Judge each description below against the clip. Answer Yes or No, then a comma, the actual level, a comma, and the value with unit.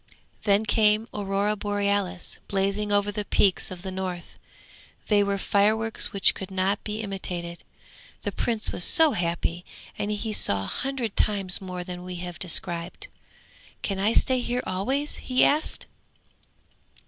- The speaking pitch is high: Yes, high, 200 Hz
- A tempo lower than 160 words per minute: Yes, average, 150 wpm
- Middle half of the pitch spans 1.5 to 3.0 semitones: Yes, narrow, 2.6 semitones